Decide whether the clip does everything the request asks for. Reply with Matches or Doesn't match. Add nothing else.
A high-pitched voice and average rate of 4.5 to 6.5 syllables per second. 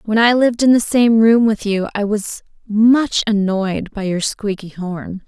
Doesn't match